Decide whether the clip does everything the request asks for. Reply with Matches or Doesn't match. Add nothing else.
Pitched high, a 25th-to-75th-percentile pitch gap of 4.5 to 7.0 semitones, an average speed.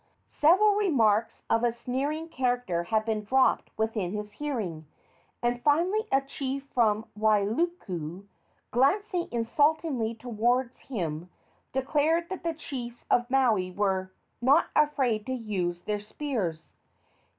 Doesn't match